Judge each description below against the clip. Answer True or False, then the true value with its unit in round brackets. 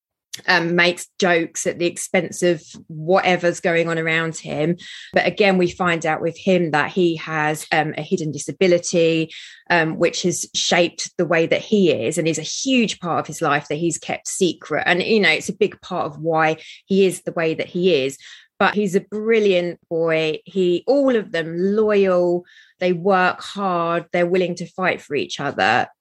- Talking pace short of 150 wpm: False (190 wpm)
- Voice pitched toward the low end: False (175 Hz)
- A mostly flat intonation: True (2.3 semitones)